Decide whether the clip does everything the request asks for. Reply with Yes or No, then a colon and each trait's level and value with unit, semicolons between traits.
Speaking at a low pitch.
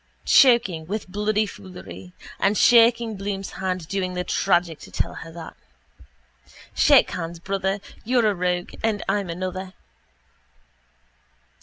No: high, 190 Hz